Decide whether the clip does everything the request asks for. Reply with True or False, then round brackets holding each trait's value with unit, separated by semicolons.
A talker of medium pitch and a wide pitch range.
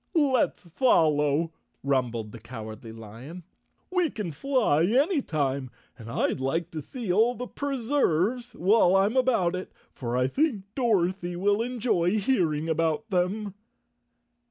True (180 Hz; 8.4 semitones)